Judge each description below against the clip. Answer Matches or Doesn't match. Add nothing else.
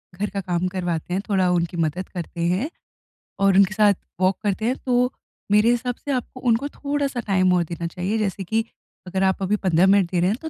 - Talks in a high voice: Matches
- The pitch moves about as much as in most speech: Matches